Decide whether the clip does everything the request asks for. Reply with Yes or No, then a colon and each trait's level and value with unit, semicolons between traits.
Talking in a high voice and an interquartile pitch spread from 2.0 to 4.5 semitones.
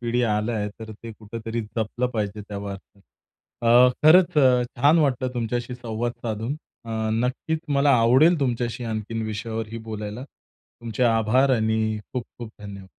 No: low, 115 Hz; narrow, 2.4 semitones